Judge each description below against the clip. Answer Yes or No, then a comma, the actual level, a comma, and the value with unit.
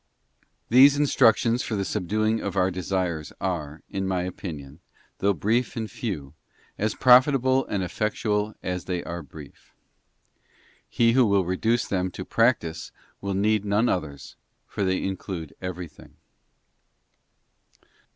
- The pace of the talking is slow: Yes, slow, 130 wpm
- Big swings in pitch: No, average, 3.8 semitones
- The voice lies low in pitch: Yes, very low, 95 Hz